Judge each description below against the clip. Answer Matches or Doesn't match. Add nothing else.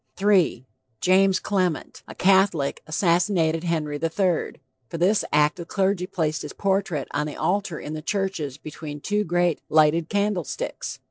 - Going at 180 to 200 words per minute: Doesn't match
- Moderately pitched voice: Matches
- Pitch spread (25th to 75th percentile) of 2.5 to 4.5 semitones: Matches